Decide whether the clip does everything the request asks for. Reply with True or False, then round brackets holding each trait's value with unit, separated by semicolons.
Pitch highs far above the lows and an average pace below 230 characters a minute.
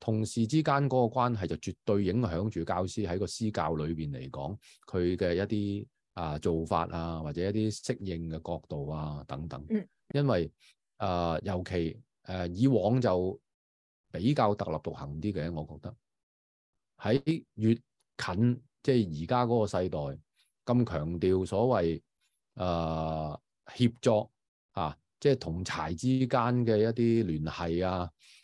True (6.3 semitones; 215 characters per minute)